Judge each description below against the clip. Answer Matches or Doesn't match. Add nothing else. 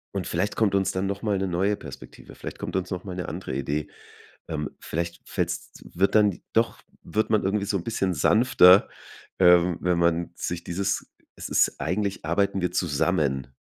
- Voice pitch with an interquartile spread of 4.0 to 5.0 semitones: Doesn't match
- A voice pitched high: Doesn't match